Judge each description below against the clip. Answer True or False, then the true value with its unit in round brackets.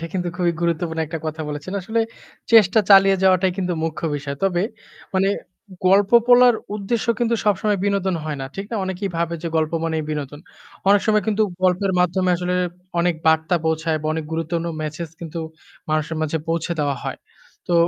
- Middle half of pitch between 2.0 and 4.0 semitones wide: True (3.4 semitones)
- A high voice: False (175 Hz)